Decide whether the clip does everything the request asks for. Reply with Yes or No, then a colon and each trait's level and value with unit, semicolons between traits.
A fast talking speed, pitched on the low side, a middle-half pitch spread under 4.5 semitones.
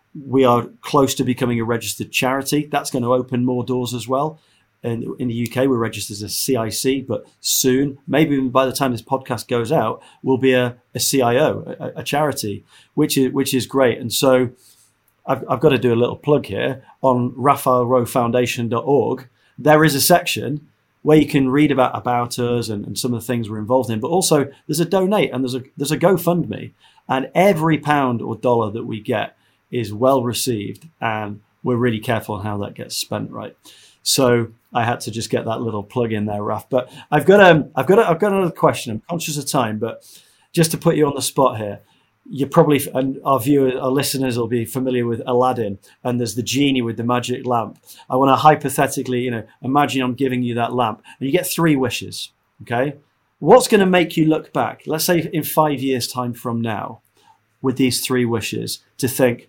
Yes: fast, 210 wpm; low, 130 Hz; average, 3.1 semitones